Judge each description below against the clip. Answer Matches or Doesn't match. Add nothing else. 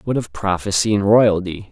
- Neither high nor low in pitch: Doesn't match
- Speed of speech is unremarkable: Matches